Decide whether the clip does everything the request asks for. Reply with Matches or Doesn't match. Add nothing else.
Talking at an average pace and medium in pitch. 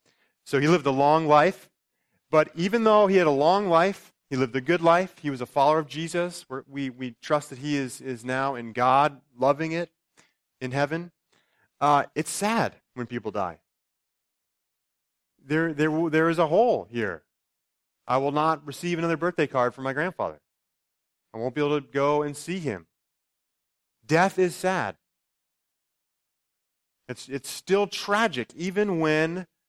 Matches